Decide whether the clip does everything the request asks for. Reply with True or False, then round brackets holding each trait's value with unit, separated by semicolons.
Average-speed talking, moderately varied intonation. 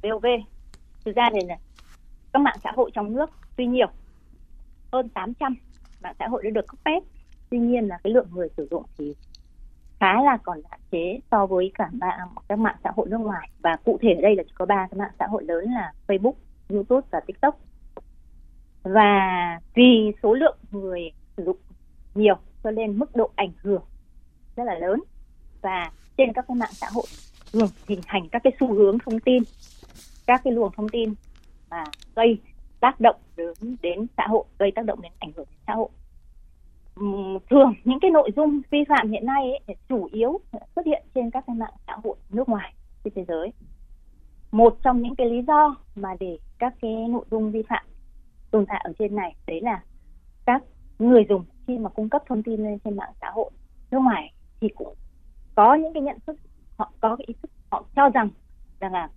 True (205 wpm; 4.7 semitones)